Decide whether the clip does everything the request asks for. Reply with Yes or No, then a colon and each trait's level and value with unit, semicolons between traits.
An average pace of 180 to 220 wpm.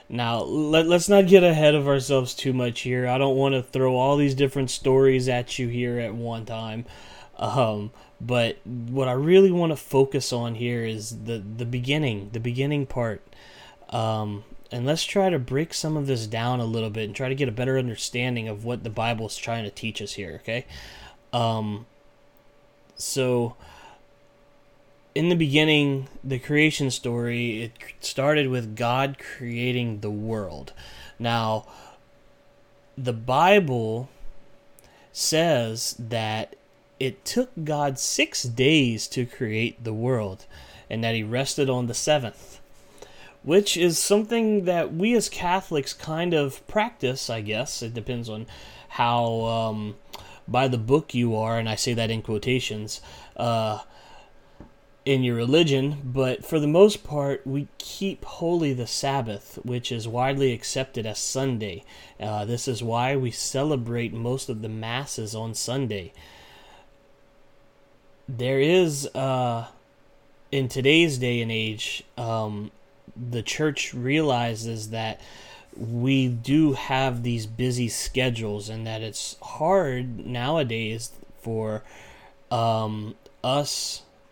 No: average, 140 wpm